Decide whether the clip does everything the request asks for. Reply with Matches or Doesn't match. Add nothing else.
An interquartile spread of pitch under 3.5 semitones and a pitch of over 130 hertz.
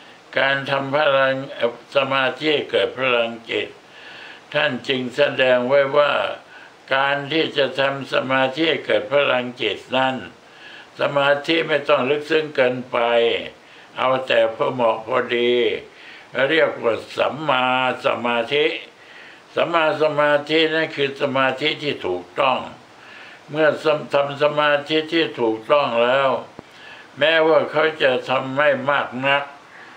Matches